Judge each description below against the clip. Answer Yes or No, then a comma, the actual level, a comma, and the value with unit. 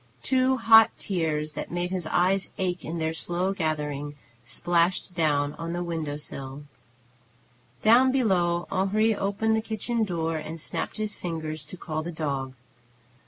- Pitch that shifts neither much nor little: Yes, average, 4.1 semitones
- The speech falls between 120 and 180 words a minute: Yes, average, 150 wpm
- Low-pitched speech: No, medium, 175 Hz